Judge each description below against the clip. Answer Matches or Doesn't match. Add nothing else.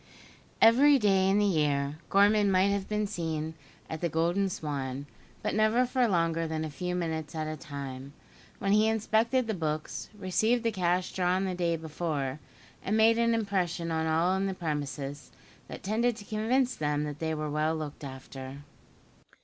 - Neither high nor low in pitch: Matches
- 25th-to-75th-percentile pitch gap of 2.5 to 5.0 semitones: Doesn't match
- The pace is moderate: Matches